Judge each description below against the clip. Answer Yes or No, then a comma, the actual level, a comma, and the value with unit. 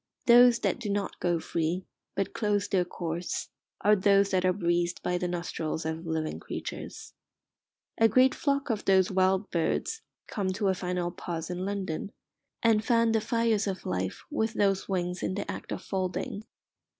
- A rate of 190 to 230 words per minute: No, average, 175 wpm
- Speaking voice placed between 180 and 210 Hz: Yes, high, 190 Hz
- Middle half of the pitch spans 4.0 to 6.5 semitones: No, average, 3.2 semitones